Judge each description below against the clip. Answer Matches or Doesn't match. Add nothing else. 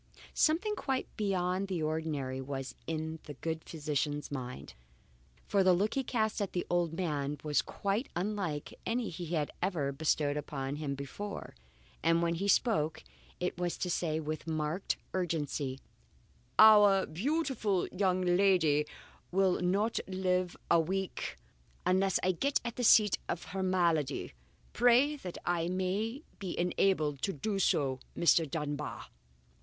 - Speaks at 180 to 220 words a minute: Doesn't match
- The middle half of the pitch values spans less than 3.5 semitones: Doesn't match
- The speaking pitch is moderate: Matches